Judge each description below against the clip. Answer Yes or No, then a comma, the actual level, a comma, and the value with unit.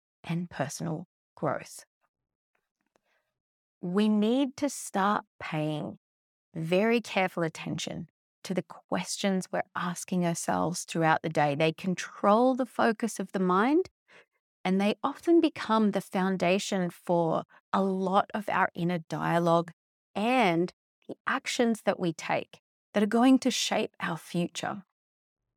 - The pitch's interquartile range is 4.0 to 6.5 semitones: Yes, average, 4.5 semitones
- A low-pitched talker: No, high, 190 Hz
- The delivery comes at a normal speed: No, slow, 125 wpm